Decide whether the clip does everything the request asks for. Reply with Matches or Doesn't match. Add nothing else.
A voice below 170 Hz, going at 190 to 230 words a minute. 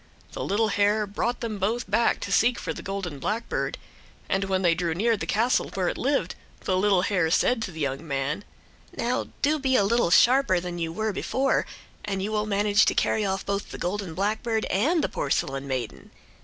Doesn't match